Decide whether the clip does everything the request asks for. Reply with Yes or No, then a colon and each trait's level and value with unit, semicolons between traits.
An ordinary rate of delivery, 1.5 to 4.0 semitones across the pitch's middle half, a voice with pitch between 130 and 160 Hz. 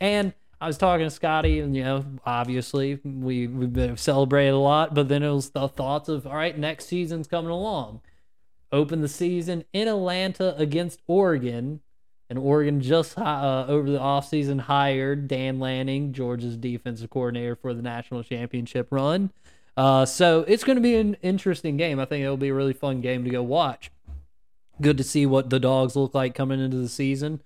Yes: average, 190 wpm; average, 3.6 semitones; medium, 140 Hz